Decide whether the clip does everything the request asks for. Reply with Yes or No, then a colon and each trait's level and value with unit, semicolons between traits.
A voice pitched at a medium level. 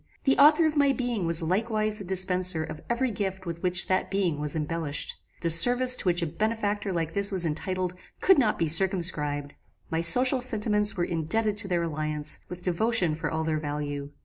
Yes: medium, 180 Hz